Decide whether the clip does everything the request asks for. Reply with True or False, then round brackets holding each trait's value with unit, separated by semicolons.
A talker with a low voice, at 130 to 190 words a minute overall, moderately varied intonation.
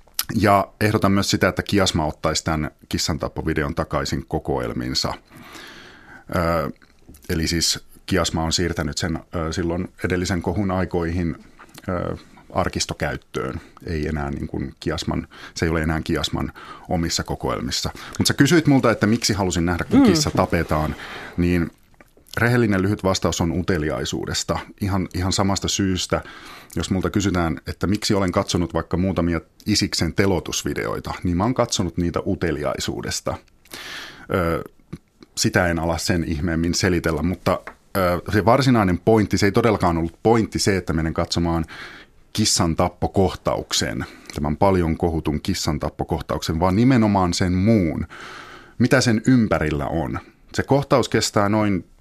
True (90 Hz; 135 wpm; 3.6 semitones)